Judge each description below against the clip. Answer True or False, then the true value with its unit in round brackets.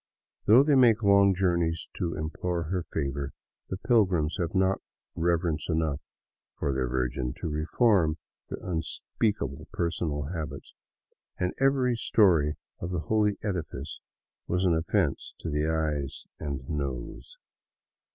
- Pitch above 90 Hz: False (85 Hz)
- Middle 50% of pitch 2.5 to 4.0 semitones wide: False (4.4 semitones)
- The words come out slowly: True (130 wpm)